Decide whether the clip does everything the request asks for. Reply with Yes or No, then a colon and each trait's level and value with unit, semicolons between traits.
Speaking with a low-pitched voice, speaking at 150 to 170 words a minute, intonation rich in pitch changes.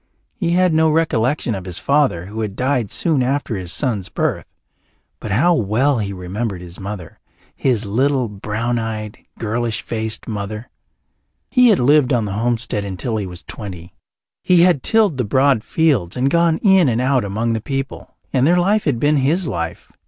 No: low, 120 Hz; average, 180 wpm; wide, 5.8 semitones